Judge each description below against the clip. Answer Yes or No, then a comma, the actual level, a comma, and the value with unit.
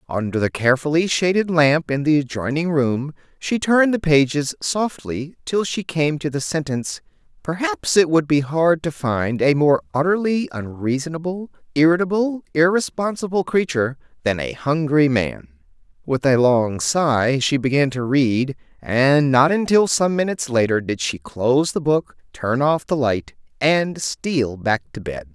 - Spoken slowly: No, average, 155 wpm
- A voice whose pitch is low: No, medium, 145 Hz